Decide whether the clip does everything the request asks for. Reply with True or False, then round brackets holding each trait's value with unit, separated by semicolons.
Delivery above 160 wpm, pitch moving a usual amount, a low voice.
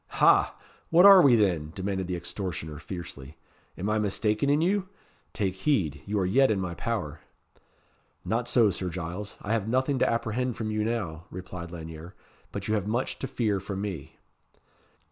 True (175 wpm; 4.6 semitones; 100 Hz)